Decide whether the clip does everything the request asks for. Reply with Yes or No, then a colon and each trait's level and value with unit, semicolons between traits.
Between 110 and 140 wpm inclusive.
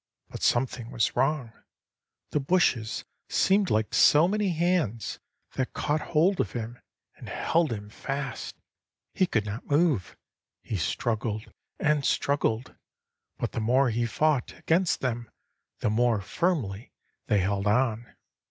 Yes: slow, 135 wpm